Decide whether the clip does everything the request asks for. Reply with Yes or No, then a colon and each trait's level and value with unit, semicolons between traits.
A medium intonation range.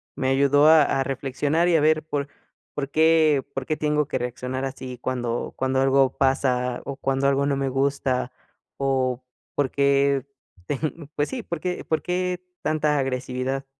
No: narrow, 2.3 semitones